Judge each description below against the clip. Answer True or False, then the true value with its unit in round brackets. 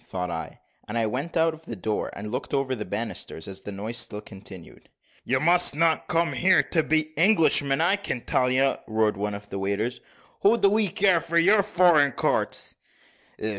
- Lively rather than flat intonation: True (8.0 semitones)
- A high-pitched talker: False (135 Hz)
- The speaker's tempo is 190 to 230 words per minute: True (195 wpm)